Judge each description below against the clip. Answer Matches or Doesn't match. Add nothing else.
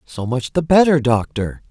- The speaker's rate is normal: Matches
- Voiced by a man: Matches